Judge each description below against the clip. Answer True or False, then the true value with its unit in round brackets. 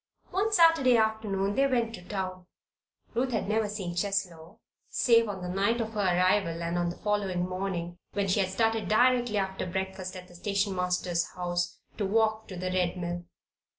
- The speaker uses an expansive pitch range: False (3.4 semitones)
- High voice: True (195 Hz)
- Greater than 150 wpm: True (185 wpm)